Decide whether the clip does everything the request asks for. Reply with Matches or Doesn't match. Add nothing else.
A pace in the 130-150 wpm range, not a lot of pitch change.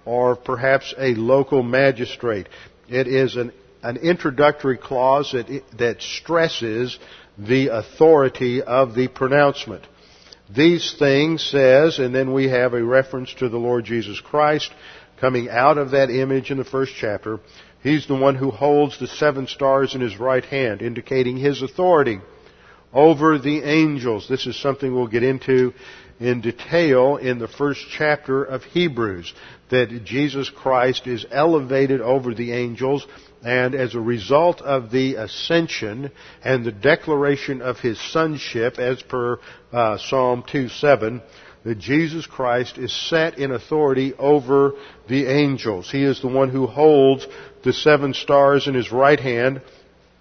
Matches